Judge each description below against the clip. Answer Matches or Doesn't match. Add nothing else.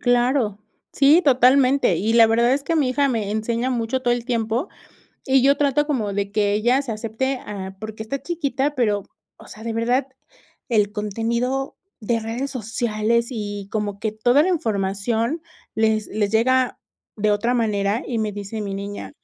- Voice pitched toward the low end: Doesn't match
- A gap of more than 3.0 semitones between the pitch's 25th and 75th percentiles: Matches